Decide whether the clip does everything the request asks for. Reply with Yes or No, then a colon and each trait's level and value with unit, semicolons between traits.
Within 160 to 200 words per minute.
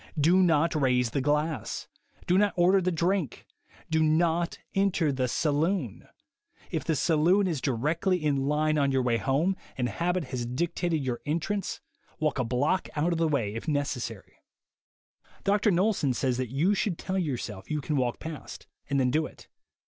Yes: average, 175 wpm